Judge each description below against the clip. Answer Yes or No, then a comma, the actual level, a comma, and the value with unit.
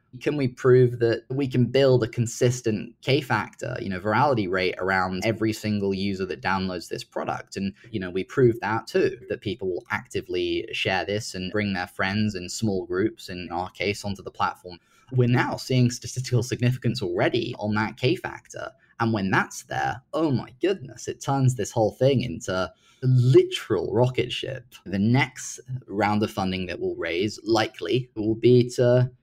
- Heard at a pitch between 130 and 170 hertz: No, low, 115 Hz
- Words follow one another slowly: No, average, 180 wpm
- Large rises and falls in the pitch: No, average, 4.0 semitones